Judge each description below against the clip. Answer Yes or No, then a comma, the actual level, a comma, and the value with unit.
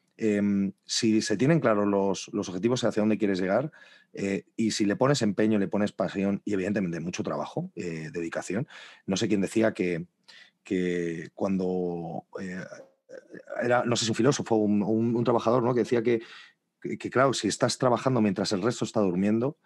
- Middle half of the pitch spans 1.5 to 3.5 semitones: Yes, average, 2.9 semitones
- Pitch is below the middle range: Yes, low, 105 Hz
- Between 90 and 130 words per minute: No, average, 185 wpm